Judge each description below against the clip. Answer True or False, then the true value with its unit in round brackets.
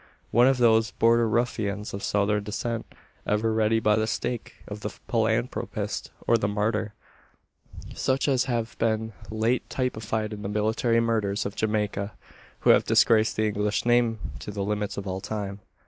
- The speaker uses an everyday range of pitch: False (1.8 semitones)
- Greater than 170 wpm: False (165 wpm)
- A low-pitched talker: True (110 Hz)